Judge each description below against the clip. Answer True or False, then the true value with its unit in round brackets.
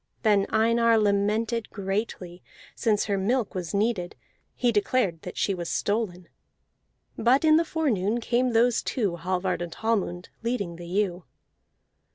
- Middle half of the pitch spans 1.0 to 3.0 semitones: False (4.2 semitones)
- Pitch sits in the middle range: False (205 Hz)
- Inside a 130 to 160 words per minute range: True (140 wpm)